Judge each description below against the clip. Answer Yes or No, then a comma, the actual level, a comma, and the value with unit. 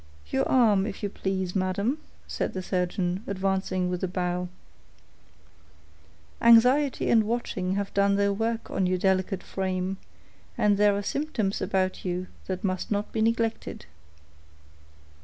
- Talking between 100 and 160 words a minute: Yes, average, 140 wpm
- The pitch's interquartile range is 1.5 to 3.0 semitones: Yes, narrow, 2.6 semitones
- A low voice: No, high, 195 Hz